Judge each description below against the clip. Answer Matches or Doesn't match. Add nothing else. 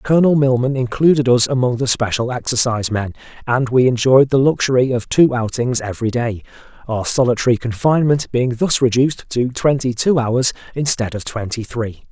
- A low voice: Matches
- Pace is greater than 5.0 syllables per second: Matches